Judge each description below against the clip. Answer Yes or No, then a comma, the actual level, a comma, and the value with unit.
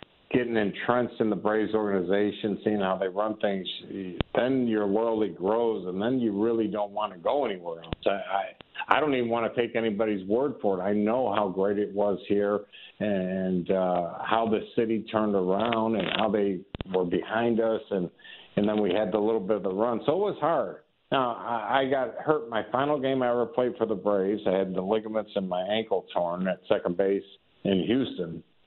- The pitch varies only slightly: Yes, narrow, 2.3 semitones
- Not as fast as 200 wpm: No, fast, 205 wpm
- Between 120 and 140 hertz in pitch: No, low, 105 Hz